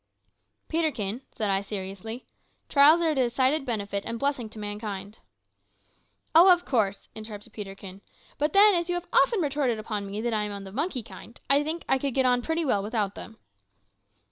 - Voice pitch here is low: No, high, 235 Hz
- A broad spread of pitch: Yes, wide, 6.0 semitones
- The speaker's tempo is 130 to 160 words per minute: No, average, 195 wpm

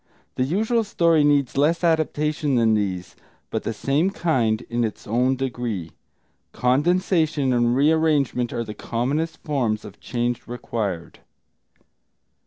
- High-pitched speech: No, low, 130 Hz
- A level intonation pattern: No, average, 5.1 semitones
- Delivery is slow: Yes, slow, 125 wpm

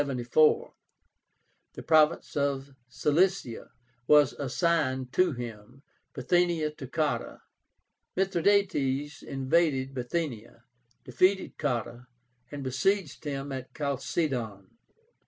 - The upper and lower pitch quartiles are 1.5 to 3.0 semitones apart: No, average, 4.0 semitones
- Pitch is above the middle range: No, medium, 140 Hz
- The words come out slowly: Yes, slow, 80 wpm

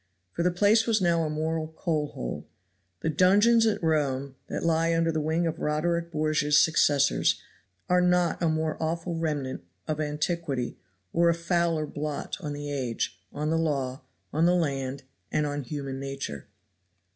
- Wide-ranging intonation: No, narrow, 2.6 semitones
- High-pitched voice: No, medium, 155 Hz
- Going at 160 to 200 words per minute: Yes, average, 165 wpm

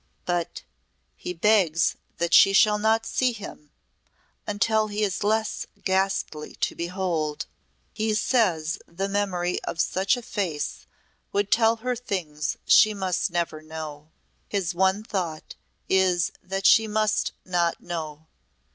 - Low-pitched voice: No, high, 190 Hz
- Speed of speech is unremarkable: No, slow, 130 wpm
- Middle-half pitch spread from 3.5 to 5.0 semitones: Yes, average, 3.9 semitones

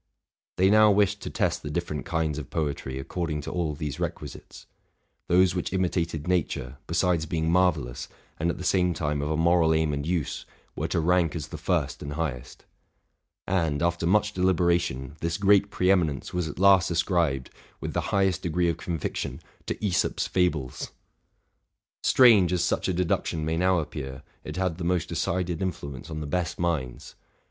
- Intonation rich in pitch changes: No, average, 3.1 semitones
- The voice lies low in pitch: Yes, very low, 85 Hz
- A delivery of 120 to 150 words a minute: No, average, 175 wpm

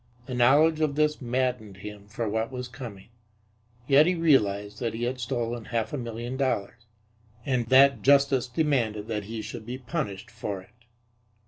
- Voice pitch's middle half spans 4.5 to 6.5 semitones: No, average, 3.7 semitones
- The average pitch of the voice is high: No, low, 120 Hz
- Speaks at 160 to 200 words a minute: Yes, average, 165 wpm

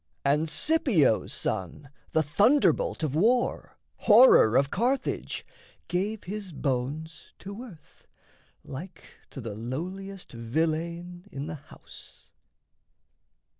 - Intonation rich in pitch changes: Yes, wide, 6.5 semitones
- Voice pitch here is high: No, medium, 165 Hz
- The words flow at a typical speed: No, slow, 100 wpm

